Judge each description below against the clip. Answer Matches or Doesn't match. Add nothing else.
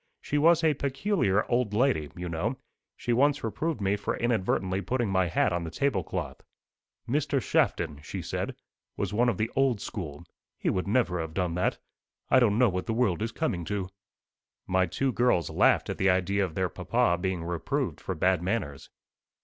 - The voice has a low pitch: Matches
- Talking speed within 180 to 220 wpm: Matches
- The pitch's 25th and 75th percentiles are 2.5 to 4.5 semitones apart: Doesn't match